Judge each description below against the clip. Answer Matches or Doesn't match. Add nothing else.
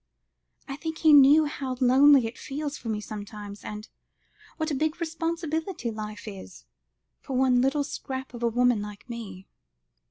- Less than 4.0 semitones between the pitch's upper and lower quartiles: Doesn't match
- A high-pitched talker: Matches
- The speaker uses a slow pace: Doesn't match